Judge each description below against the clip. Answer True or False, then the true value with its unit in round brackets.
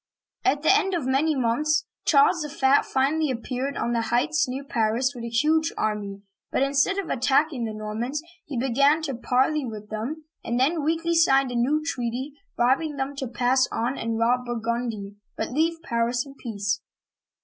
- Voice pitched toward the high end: True (265 Hz)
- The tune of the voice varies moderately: True (4.2 semitones)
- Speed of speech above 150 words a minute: True (180 wpm)